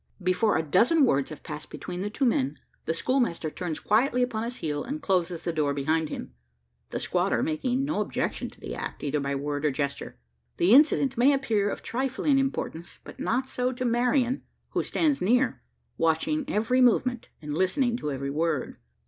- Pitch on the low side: No, high, 205 Hz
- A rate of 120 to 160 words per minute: No, average, 185 wpm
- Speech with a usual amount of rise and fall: No, wide, 8.5 semitones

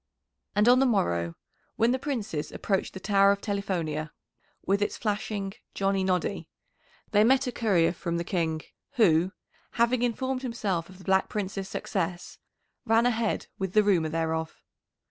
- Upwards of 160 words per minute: No, average, 155 wpm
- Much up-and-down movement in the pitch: No, average, 4.7 semitones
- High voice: Yes, high, 195 Hz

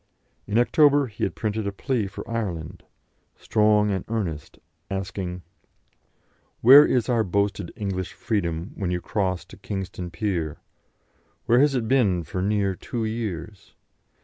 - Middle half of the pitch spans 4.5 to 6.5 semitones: No, average, 3.7 semitones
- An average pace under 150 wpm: Yes, average, 140 wpm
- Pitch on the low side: Yes, low, 100 Hz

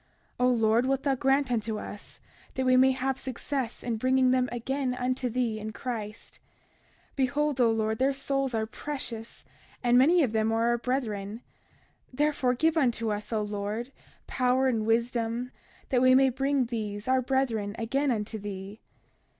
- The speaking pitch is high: Yes, very high, 250 Hz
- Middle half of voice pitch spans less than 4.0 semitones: Yes, average, 3.1 semitones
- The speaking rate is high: No, average, 170 wpm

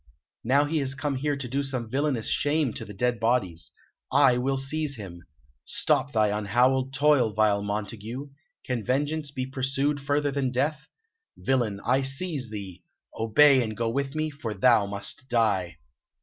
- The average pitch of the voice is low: Yes, low, 130 Hz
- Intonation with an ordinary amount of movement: Yes, average, 4.3 semitones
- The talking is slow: No, average, 165 wpm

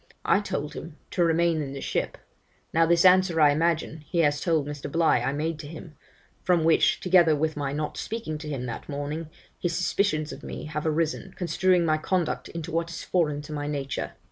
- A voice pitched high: No, medium, 160 Hz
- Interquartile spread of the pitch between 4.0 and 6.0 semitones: No, narrow, 2.4 semitones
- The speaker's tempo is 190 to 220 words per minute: Yes, fast, 205 wpm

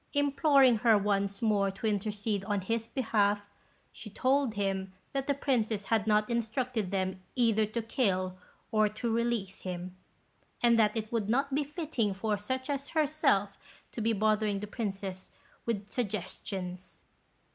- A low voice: No, high, 215 Hz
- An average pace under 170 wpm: Yes, average, 150 wpm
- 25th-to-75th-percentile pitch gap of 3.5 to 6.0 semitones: No, average, 3.1 semitones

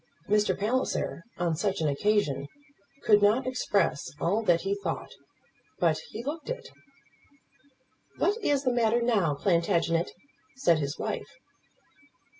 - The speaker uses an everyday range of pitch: No, wide, 6.3 semitones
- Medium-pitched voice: No, high, 205 Hz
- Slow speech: Yes, slow, 125 wpm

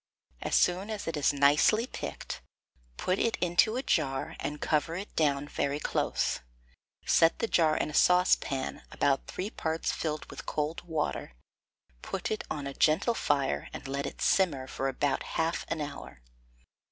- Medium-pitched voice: Yes, medium, 155 Hz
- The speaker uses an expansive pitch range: No, average, 4.2 semitones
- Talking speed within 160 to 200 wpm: Yes, average, 165 wpm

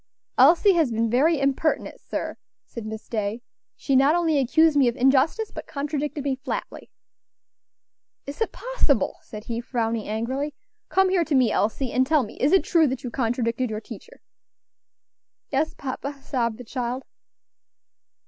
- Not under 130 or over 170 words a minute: Yes, average, 160 wpm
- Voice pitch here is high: Yes, very high, 270 Hz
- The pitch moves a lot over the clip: No, average, 4.4 semitones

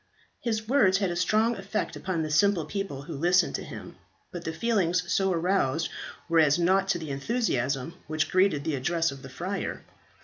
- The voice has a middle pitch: Yes, medium, 175 Hz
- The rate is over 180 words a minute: Yes, average, 190 wpm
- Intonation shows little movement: No, average, 4.1 semitones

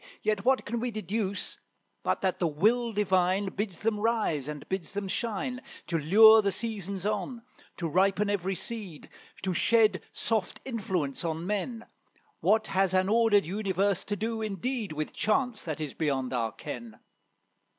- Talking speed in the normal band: Yes, average, 160 wpm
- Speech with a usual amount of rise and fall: Yes, average, 3.8 semitones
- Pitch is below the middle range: No, high, 200 Hz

